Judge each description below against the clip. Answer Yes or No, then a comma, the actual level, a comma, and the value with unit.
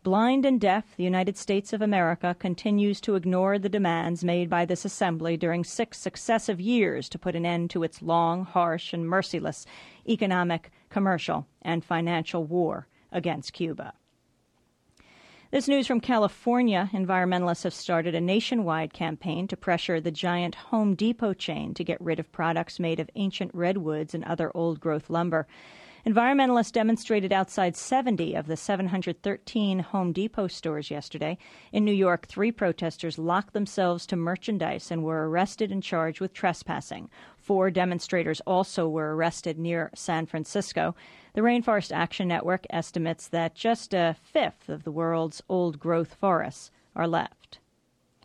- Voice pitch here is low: No, medium, 180 Hz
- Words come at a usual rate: Yes, average, 150 wpm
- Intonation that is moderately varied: Yes, average, 3.3 semitones